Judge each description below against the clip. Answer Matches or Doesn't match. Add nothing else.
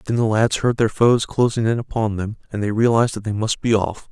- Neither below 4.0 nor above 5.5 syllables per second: Doesn't match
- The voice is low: Matches